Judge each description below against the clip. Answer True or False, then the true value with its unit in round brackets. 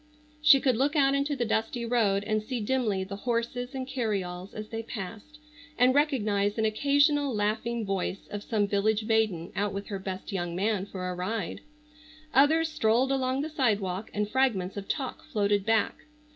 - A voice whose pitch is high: True (220 Hz)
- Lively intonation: False (4.6 semitones)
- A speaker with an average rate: True (175 wpm)